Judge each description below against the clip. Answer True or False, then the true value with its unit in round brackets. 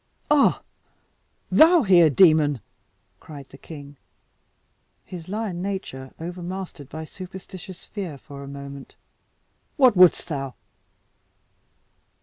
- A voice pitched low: False (170 Hz)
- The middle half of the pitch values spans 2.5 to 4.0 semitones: False (5.1 semitones)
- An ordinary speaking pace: False (100 wpm)